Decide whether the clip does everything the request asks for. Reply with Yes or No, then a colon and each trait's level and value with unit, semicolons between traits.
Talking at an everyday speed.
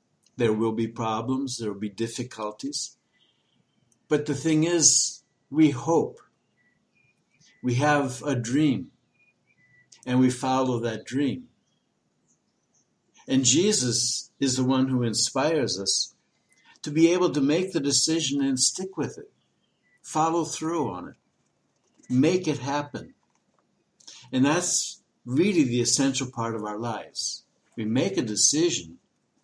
No: slow, 125 wpm